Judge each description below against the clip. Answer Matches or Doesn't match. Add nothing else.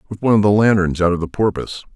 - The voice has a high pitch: Doesn't match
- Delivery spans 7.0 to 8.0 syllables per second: Matches